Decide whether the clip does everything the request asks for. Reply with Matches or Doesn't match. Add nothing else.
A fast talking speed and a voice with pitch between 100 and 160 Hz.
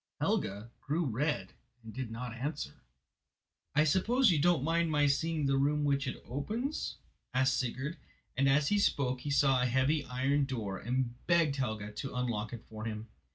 Doesn't match